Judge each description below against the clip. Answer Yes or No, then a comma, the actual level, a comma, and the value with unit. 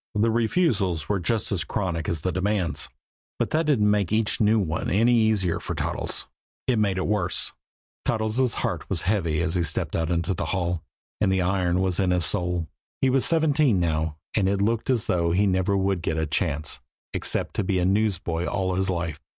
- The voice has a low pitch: Yes, very low, 95 Hz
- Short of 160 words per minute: No, average, 200 wpm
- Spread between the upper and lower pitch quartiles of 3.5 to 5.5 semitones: Yes, average, 3.8 semitones